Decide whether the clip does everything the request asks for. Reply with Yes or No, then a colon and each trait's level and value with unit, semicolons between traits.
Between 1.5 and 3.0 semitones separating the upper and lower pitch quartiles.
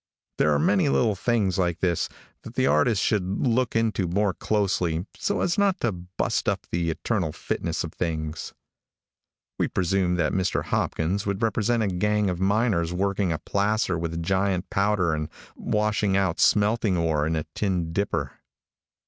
No: average, 3.7 semitones